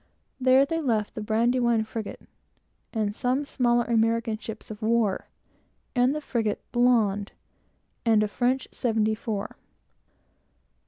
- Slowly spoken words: Yes, slow, 125 wpm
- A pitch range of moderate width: No, narrow, 2.3 semitones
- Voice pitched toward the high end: Yes, high, 230 Hz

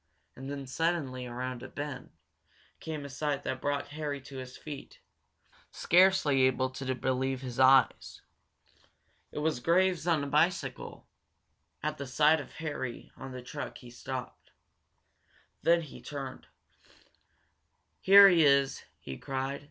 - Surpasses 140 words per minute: No, slow, 135 wpm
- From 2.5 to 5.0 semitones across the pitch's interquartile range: Yes, average, 2.8 semitones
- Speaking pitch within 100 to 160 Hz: Yes, medium, 140 Hz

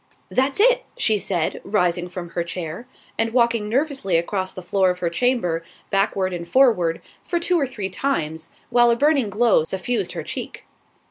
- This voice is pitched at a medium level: No, high, 200 Hz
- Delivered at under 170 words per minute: No, average, 175 wpm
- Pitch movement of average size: No, wide, 5.7 semitones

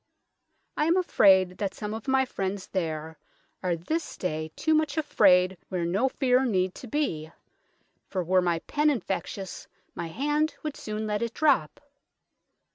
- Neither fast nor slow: Yes, average, 155 wpm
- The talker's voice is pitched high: Yes, high, 205 Hz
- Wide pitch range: Yes, wide, 7.3 semitones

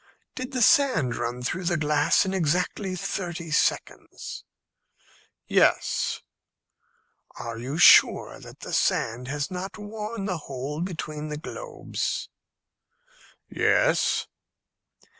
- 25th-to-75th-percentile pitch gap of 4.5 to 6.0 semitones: Yes, average, 5.1 semitones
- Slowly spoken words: Yes, slow, 105 wpm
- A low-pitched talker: No, medium, 170 Hz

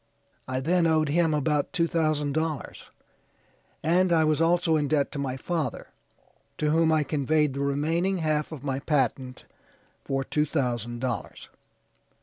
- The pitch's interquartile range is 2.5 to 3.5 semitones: Yes, average, 2.8 semitones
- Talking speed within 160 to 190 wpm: No, average, 150 wpm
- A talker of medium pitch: Yes, medium, 150 Hz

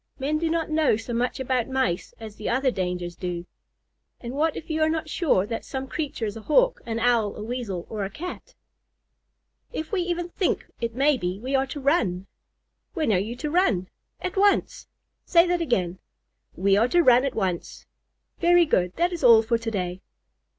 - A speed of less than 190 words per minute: No, average, 200 wpm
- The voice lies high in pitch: Yes, very high, 250 Hz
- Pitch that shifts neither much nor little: No, wide, 7.2 semitones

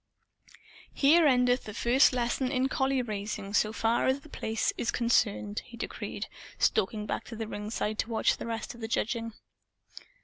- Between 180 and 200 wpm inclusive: No, average, 170 wpm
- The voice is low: No, high, 230 Hz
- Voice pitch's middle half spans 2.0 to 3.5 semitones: Yes, average, 2.9 semitones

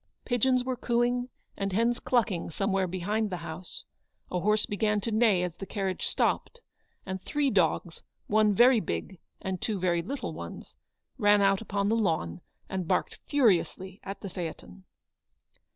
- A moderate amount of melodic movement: Yes, average, 3.8 semitones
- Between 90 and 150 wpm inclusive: No, average, 160 wpm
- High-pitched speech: Yes, high, 200 Hz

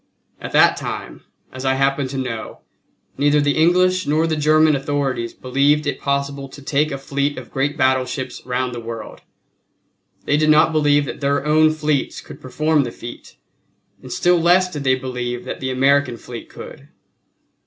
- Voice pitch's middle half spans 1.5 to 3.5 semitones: Yes, average, 2.7 semitones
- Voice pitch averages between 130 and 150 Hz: Yes, medium, 140 Hz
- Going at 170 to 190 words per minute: Yes, average, 175 wpm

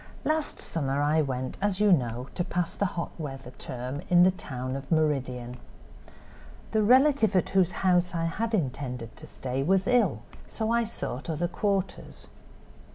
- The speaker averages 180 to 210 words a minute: No, average, 160 wpm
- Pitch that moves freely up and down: Yes, wide, 6.6 semitones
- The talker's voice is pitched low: No, medium, 165 Hz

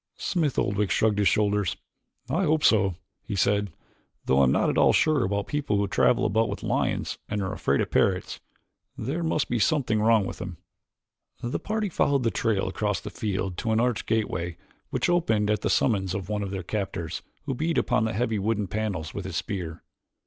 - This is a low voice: Yes, low, 105 Hz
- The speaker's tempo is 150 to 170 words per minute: No, average, 200 wpm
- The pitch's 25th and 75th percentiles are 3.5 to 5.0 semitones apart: Yes, average, 3.9 semitones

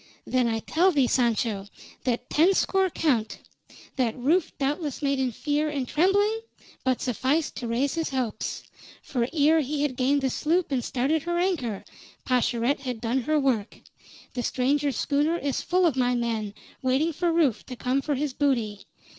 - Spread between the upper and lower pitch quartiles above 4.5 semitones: No, average, 3.9 semitones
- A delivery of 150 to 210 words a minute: Yes, average, 170 wpm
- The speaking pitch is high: Yes, very high, 270 Hz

